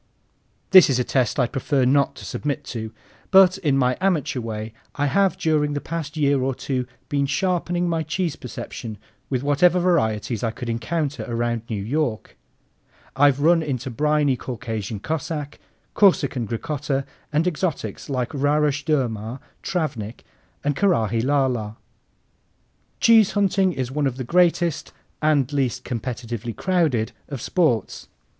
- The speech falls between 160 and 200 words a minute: No, average, 145 wpm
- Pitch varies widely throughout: No, average, 4.8 semitones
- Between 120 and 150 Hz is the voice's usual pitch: Yes, medium, 140 Hz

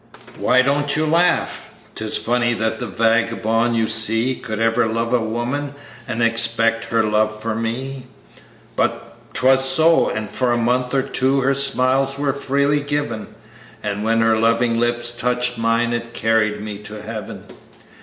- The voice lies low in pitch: Yes, low, 120 Hz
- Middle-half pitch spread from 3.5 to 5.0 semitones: No, average, 2.8 semitones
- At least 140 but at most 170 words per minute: Yes, average, 160 wpm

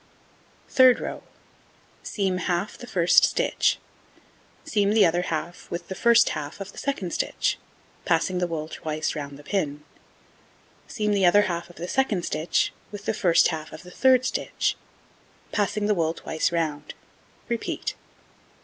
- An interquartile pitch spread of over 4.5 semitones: No, average, 4.2 semitones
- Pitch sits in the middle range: Yes, medium, 180 Hz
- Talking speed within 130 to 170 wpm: Yes, average, 155 wpm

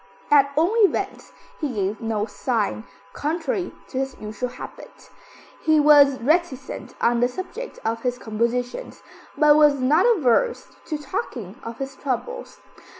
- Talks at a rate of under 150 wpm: Yes, average, 140 wpm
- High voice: Yes, very high, 270 Hz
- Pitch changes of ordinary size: Yes, average, 4.5 semitones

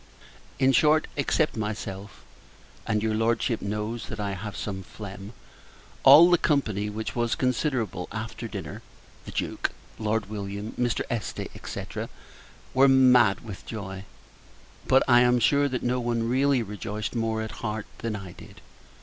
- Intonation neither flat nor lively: Yes, average, 3.3 semitones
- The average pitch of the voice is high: No, low, 110 Hz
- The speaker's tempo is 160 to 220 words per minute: No, average, 150 wpm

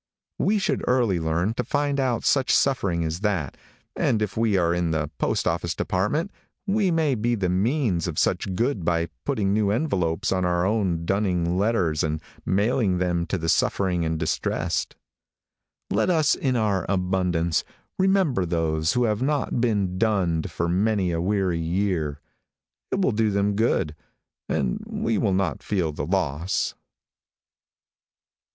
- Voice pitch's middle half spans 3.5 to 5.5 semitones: Yes, average, 5.1 semitones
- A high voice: No, very low, 95 Hz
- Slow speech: No, average, 155 wpm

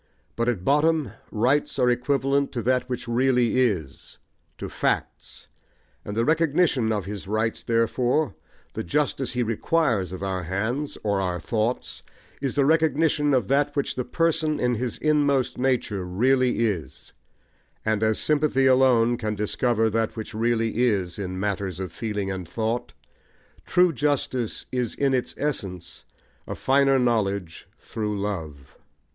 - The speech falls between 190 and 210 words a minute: No, average, 145 wpm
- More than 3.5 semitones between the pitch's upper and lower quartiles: Yes, average, 4.7 semitones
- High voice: No, low, 120 Hz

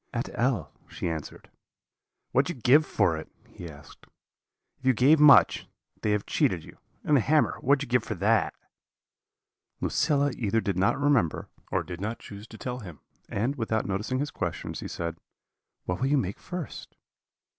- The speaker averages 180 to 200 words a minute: Yes, average, 185 wpm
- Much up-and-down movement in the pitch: Yes, wide, 6.4 semitones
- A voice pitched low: Yes, low, 115 Hz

